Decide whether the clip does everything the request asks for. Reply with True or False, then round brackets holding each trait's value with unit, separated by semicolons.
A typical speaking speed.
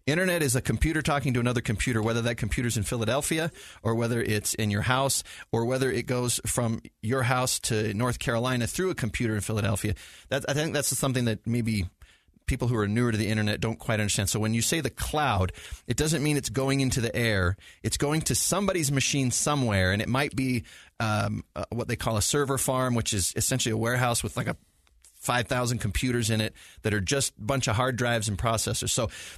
False (215 wpm)